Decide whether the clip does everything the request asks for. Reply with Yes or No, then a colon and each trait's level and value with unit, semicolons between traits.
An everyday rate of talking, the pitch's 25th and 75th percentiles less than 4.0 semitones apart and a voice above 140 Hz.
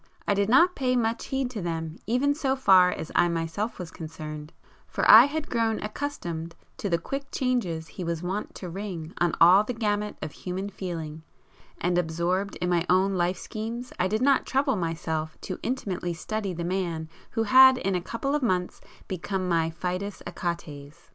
No: average, 185 wpm; average, 5.2 semitones; medium, 185 Hz